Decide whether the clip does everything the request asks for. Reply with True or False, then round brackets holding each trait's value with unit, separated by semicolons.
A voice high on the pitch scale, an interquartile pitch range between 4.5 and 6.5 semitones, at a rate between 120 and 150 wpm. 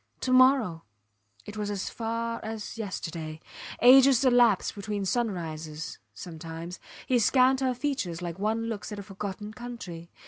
True (210 Hz; 5.5 semitones; 140 wpm)